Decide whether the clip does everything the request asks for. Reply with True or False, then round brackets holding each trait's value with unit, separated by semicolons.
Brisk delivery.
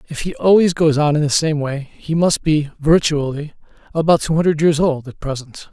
True (210 wpm)